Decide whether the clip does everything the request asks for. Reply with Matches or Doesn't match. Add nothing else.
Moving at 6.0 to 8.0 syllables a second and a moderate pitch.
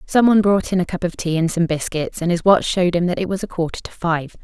Matches